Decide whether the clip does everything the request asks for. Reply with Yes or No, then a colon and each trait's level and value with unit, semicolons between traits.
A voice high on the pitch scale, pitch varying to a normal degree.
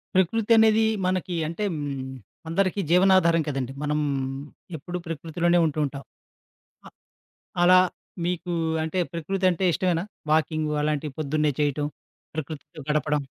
No: medium, 165 Hz; average, 3.5 semitones